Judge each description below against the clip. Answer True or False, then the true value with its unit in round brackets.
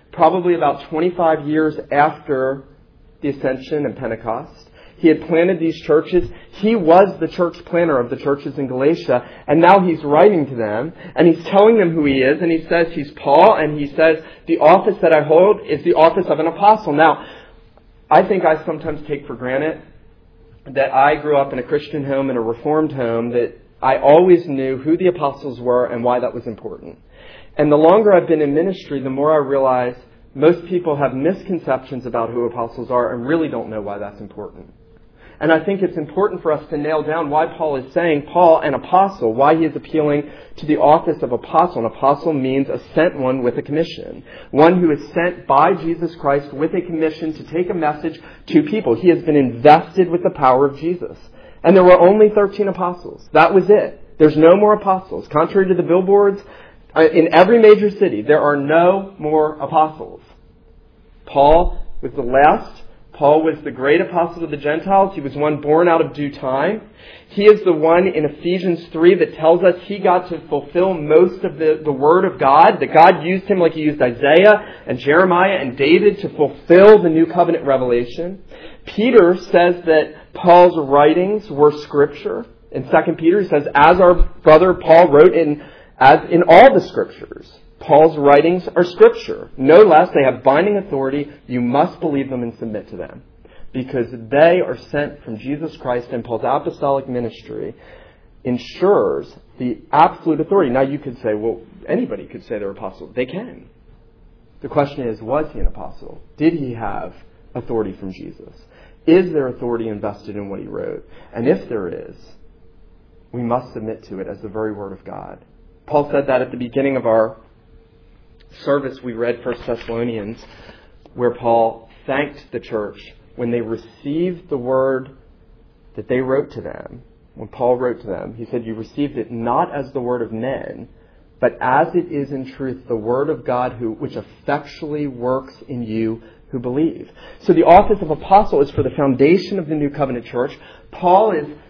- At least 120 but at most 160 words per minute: False (185 wpm)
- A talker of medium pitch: True (150 Hz)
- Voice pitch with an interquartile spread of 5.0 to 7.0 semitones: True (5.3 semitones)